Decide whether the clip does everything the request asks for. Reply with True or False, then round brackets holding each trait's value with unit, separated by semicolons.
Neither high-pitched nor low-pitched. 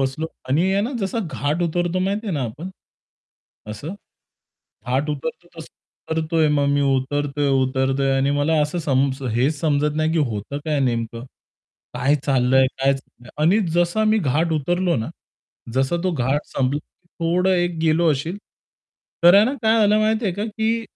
True (155 Hz)